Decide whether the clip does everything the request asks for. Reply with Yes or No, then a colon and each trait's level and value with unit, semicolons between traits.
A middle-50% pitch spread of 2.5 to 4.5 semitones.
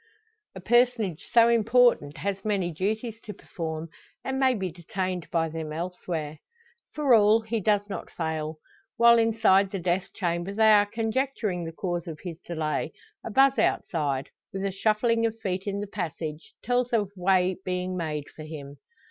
No: average, 5.0 semitones